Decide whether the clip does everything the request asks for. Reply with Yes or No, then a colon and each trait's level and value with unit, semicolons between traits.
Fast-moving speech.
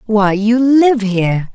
No: average, 155 wpm